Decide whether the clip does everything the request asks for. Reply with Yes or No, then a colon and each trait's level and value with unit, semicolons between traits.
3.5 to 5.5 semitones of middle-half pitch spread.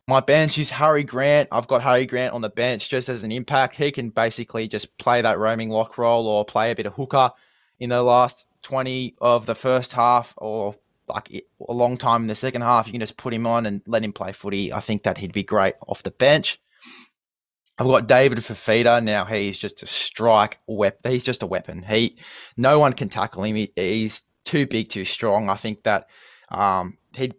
No: average, 2.9 semitones